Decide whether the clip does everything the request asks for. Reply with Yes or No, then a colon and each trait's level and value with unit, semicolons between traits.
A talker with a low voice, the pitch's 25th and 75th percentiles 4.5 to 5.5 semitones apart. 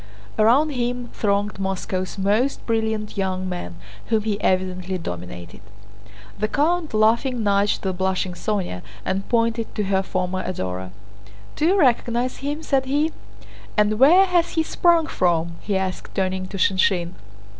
No: high, 205 Hz; average, 4.9 semitones